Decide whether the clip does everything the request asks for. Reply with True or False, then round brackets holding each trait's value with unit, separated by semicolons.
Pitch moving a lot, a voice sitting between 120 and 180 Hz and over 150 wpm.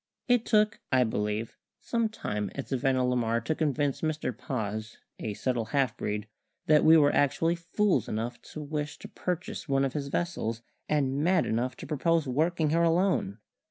True (5.8 semitones; 140 Hz; 175 wpm)